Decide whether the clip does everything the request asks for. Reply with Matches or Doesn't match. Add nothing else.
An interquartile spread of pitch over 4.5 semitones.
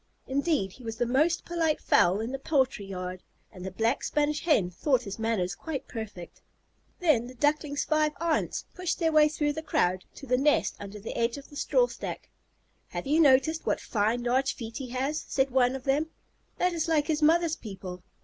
Matches